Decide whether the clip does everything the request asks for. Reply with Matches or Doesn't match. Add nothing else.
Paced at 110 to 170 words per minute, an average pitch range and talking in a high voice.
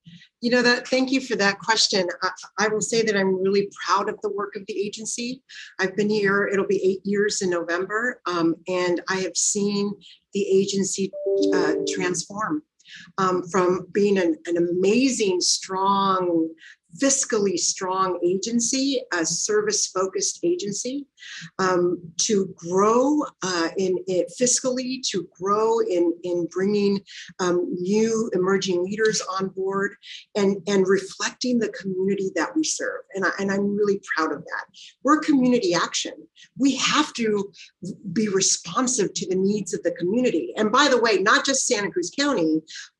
Matches